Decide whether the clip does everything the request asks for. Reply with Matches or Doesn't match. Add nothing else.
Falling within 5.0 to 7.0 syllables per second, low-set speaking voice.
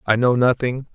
Matches